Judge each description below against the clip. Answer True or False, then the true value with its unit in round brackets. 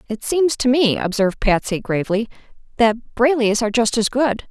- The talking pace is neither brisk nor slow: True (175 wpm)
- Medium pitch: False (235 Hz)